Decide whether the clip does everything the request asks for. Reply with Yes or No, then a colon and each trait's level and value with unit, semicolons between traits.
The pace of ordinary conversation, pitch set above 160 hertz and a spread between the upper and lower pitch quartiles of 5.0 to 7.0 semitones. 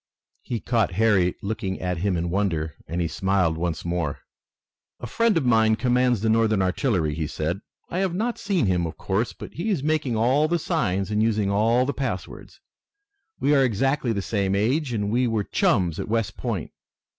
No: average, 190 wpm; low, 110 Hz; wide, 5.5 semitones